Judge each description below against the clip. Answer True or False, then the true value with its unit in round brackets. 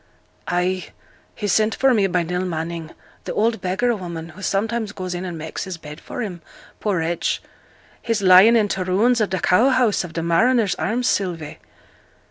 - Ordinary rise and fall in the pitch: True (4.2 semitones)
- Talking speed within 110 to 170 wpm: False (185 wpm)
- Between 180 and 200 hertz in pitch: True (185 Hz)